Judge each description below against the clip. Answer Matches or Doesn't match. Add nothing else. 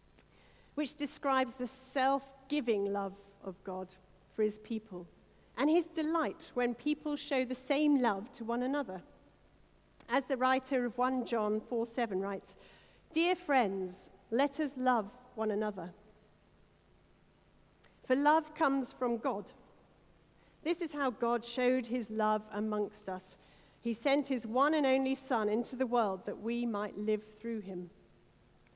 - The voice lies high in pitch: Matches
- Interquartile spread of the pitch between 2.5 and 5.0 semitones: Matches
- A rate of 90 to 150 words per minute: Matches